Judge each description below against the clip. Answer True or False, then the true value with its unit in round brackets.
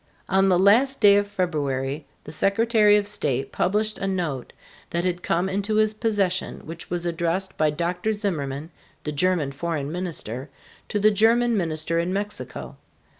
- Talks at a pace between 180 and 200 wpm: False (160 wpm)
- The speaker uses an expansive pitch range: False (4.6 semitones)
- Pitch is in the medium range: True (180 Hz)